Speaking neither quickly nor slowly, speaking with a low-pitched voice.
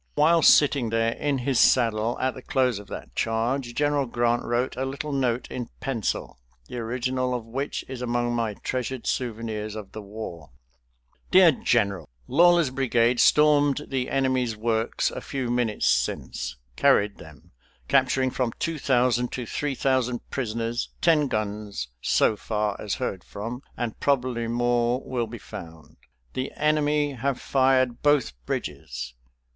Yes: average, 150 wpm; low, 120 Hz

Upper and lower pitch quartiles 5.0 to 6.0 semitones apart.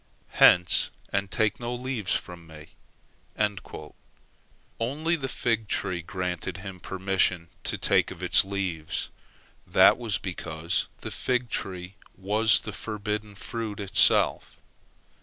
No: average, 3.8 semitones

